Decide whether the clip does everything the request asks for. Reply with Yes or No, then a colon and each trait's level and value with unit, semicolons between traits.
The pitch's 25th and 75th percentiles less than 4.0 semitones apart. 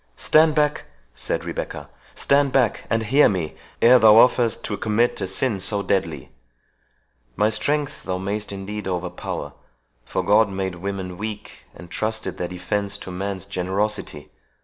Yes: average, 3.2 semitones